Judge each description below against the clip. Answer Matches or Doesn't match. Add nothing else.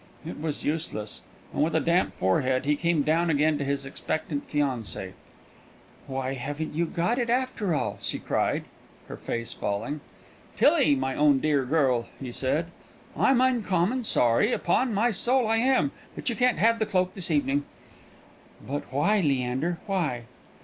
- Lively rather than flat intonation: Matches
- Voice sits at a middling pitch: Matches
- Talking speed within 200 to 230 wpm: Doesn't match